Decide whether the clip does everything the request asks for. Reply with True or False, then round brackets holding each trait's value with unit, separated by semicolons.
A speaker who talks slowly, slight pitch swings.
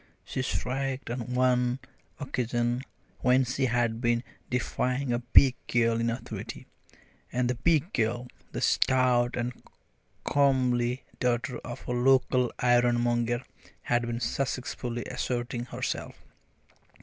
True (115 wpm; 1.1 semitones)